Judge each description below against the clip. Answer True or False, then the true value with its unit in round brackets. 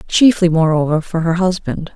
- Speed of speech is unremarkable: True (155 wpm)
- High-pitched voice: False (170 Hz)